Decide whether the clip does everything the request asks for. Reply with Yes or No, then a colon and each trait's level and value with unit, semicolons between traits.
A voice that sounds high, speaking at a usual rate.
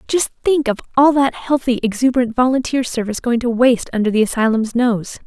Yes: high, 245 Hz; average, 180 wpm